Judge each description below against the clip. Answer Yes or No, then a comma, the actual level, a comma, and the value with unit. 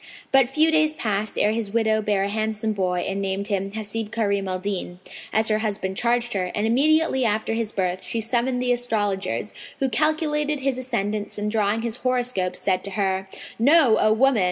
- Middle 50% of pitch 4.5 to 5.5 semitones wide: No, average, 3.7 semitones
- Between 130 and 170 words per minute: No, average, 190 wpm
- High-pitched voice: Yes, high, 220 Hz